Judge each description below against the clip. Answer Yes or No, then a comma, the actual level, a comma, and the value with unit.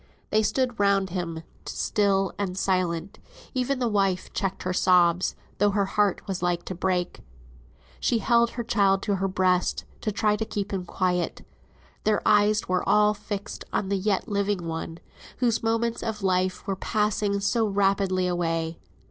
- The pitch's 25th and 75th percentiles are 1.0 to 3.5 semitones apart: Yes, narrow, 2.4 semitones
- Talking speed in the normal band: Yes, average, 165 wpm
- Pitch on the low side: No, high, 195 Hz